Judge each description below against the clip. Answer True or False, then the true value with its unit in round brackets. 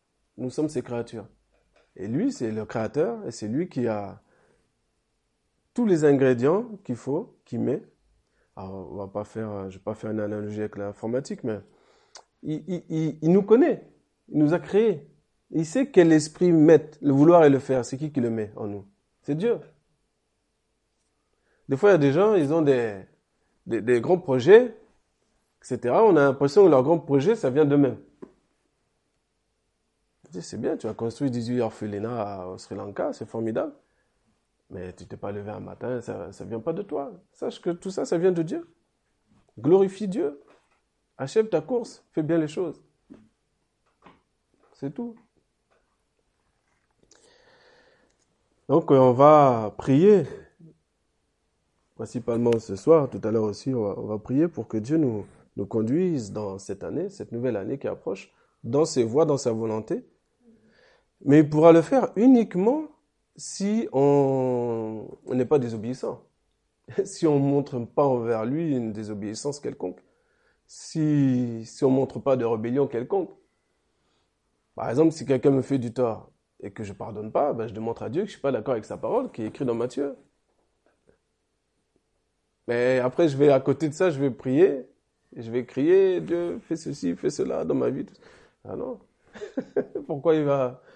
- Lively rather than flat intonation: True (6.4 semitones)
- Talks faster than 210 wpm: False (170 wpm)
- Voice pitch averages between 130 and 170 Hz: True (135 Hz)